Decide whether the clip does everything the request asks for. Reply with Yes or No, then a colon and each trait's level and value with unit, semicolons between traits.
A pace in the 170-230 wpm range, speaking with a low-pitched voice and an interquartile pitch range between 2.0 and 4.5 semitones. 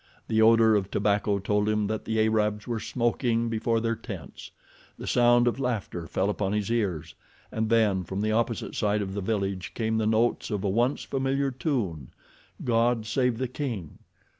Yes: average, 180 wpm; low, 110 Hz; narrow, 2.4 semitones